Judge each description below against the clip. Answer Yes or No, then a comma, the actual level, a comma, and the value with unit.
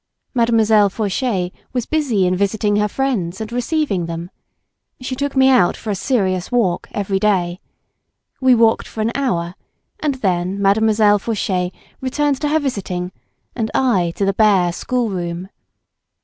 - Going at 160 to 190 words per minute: No, average, 150 wpm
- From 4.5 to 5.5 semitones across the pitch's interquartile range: Yes, average, 5.2 semitones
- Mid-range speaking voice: No, high, 210 Hz